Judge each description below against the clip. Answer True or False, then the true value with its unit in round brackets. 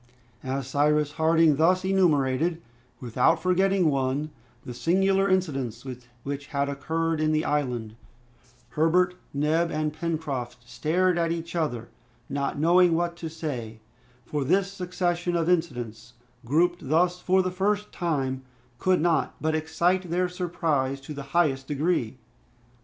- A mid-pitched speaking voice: True (160 Hz)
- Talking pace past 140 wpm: False (135 wpm)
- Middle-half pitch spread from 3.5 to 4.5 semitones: True (4.1 semitones)